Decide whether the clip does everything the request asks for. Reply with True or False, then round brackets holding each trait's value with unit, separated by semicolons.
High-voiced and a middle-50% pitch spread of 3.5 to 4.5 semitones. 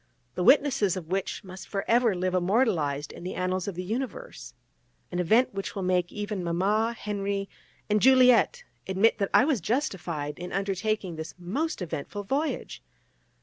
True (195 Hz; 4.0 semitones)